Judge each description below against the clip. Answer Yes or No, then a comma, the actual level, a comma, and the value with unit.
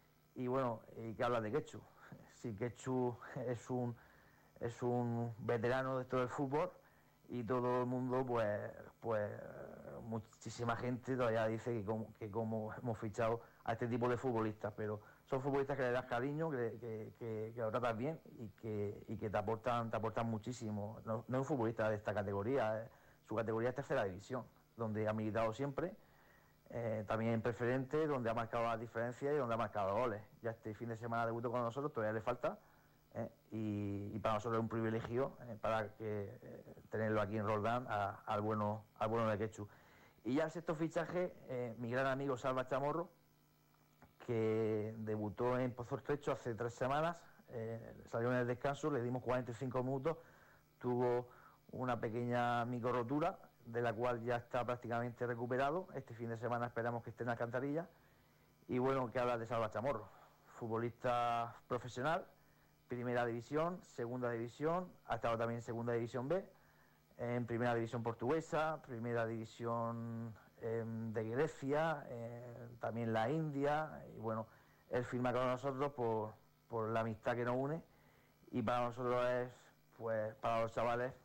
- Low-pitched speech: Yes, low, 120 Hz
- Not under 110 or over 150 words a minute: No, average, 170 wpm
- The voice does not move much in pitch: Yes, narrow, 2.1 semitones